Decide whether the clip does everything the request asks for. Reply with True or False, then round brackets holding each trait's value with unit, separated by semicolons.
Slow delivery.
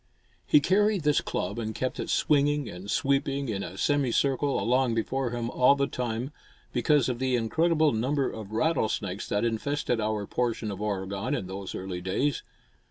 False (170 wpm)